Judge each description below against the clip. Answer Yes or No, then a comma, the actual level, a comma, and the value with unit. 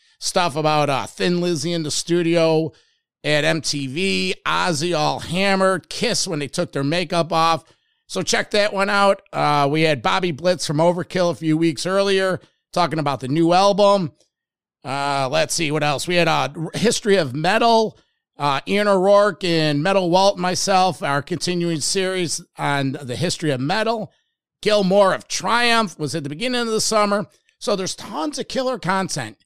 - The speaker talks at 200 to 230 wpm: No, average, 175 wpm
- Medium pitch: Yes, medium, 175 Hz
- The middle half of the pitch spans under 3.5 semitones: No, average, 4.1 semitones